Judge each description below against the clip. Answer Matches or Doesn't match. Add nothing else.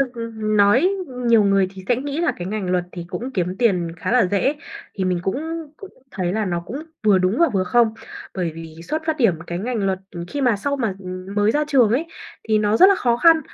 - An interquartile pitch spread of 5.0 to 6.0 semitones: Matches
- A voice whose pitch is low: Doesn't match